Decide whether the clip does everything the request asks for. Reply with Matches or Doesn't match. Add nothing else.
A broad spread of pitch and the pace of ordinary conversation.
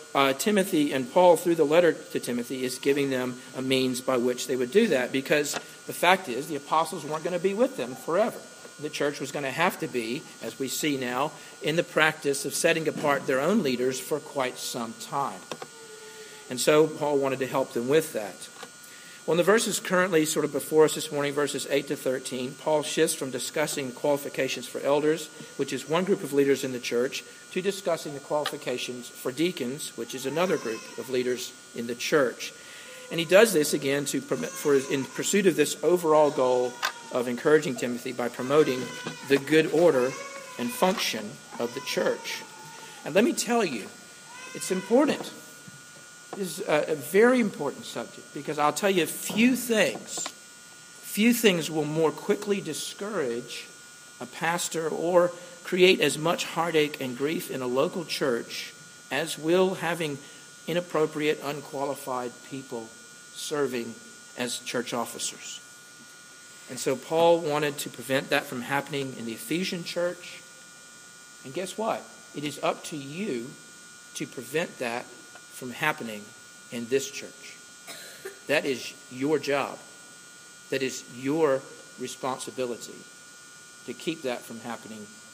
Doesn't match